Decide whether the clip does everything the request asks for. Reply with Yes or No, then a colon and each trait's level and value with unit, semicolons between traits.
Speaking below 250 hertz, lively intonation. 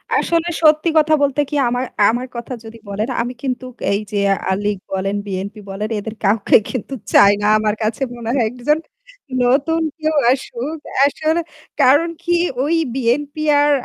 No: very high, 255 Hz; wide, 5.8 semitones